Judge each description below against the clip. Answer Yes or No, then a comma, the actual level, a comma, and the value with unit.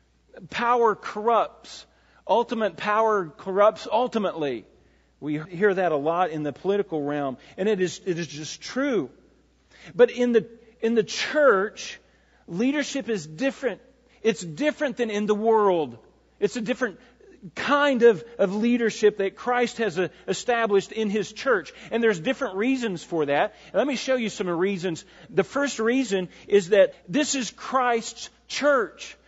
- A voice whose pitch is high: Yes, high, 215 Hz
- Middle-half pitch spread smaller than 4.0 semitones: No, average, 4.8 semitones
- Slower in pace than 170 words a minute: Yes, average, 150 wpm